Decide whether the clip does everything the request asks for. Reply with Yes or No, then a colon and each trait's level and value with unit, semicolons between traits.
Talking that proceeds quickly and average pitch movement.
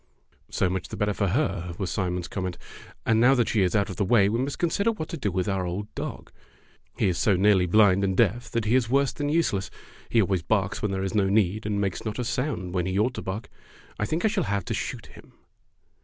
Yes: fast, 250 wpm; average, 4.0 semitones